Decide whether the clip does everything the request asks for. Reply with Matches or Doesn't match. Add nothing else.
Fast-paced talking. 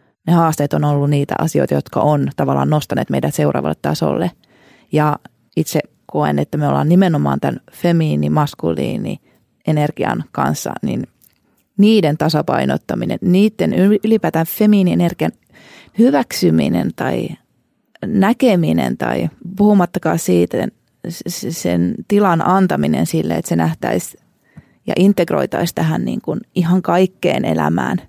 Doesn't match